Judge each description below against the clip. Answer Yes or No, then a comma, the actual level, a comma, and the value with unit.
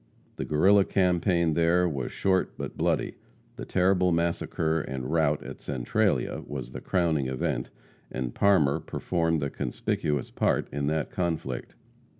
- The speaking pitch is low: Yes, very low, 80 Hz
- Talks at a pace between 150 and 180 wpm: No, average, 140 wpm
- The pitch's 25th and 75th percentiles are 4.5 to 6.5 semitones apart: No, average, 4.0 semitones